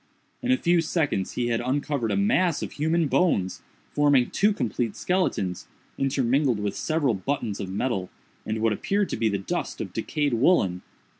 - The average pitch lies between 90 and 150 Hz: Yes, low, 135 Hz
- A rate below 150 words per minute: No, average, 170 wpm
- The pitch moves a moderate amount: No, wide, 7.1 semitones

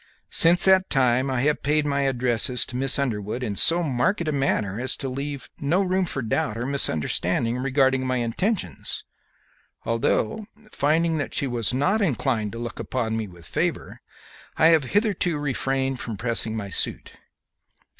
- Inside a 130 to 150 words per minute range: No, average, 165 wpm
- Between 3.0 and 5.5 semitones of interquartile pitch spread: Yes, average, 4.4 semitones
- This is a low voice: Yes, low, 130 Hz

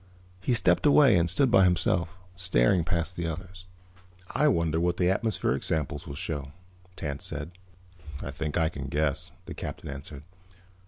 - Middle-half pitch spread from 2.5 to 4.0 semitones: Yes, average, 3.6 semitones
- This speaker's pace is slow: No, average, 160 wpm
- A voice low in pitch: Yes, very low, 85 Hz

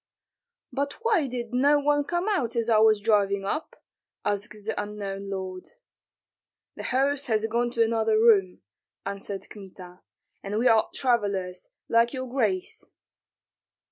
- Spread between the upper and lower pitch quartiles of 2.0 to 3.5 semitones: No, average, 4.1 semitones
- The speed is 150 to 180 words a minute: No, average, 140 wpm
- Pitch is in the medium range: No, high, 220 Hz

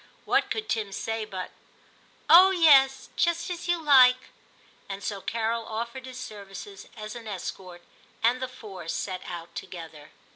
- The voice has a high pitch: Yes, high, 225 Hz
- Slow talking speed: No, average, 170 wpm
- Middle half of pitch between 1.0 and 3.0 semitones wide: No, average, 5.1 semitones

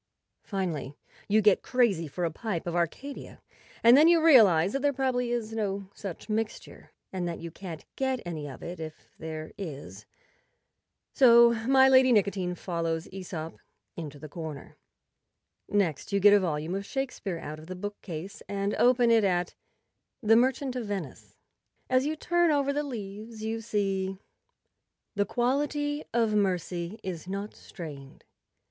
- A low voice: No, high, 200 Hz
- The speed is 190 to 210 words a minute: No, average, 165 wpm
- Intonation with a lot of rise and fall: Yes, wide, 5.9 semitones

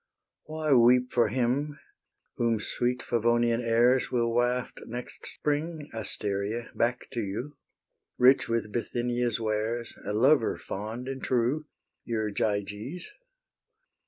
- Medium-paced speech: No, slow, 115 wpm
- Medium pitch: No, low, 120 Hz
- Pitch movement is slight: Yes, narrow, 2.1 semitones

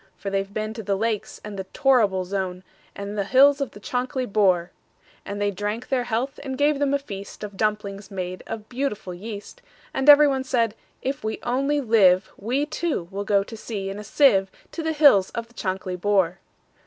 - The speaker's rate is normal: Yes, average, 180 wpm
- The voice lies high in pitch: Yes, high, 215 Hz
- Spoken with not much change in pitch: No, average, 5.1 semitones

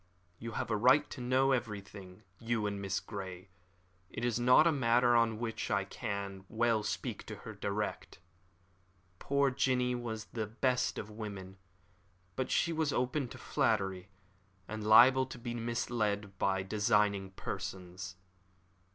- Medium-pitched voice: No, low, 110 Hz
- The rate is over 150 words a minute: No, average, 145 wpm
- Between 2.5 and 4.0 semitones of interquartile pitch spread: Yes, average, 3.6 semitones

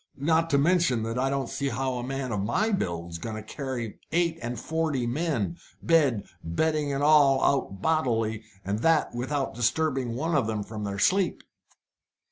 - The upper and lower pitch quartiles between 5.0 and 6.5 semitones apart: Yes, wide, 5.6 semitones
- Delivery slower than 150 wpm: No, average, 170 wpm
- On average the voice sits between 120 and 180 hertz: Yes, low, 135 Hz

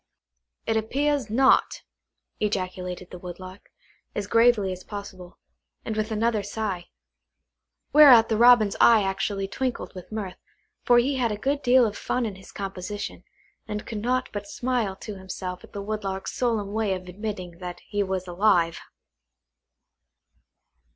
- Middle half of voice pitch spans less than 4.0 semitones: Yes, average, 3.4 semitones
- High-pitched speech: Yes, high, 205 Hz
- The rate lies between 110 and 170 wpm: Yes, average, 145 wpm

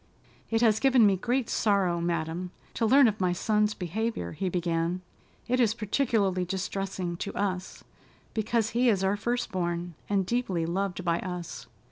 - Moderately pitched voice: No, high, 195 Hz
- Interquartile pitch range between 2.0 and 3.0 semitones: No, average, 3.9 semitones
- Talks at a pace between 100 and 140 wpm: No, average, 160 wpm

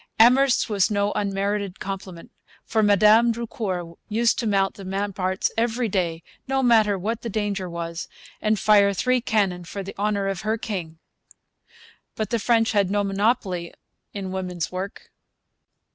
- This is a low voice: No, high, 200 Hz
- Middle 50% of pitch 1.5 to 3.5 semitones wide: Yes, average, 2.8 semitones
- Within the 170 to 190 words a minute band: No, average, 150 wpm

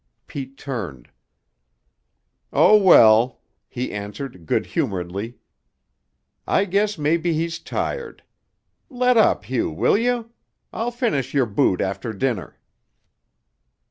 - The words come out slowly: Yes, slow, 105 wpm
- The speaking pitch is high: No, low, 135 Hz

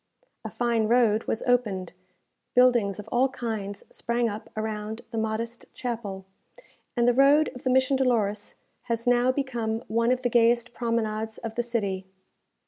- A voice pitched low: No, high, 230 Hz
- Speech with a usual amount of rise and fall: No, narrow, 2.2 semitones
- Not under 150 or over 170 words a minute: Yes, average, 155 wpm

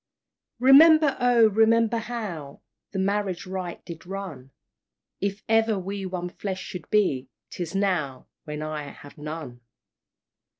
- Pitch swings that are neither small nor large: No, wide, 5.7 semitones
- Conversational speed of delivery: No, slow, 125 wpm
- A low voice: No, high, 190 Hz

